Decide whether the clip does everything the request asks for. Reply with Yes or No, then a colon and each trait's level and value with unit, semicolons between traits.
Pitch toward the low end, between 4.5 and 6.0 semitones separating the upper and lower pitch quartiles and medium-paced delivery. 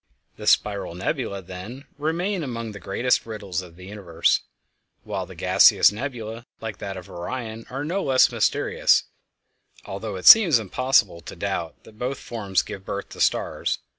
Yes: low, 110 Hz; average, 5.1 semitones; average, 160 wpm